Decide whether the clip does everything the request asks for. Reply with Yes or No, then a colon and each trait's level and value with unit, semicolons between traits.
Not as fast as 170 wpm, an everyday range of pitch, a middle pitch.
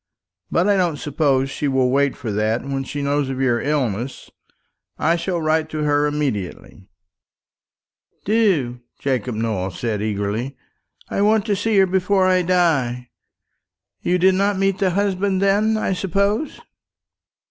No: average, 145 wpm; wide, 6.9 semitones; medium, 150 Hz